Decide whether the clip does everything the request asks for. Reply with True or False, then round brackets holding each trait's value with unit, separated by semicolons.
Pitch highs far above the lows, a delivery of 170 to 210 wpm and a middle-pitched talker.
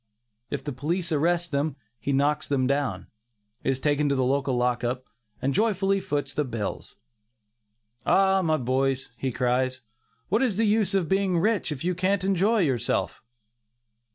False (6.1 semitones; 155 wpm; 145 Hz)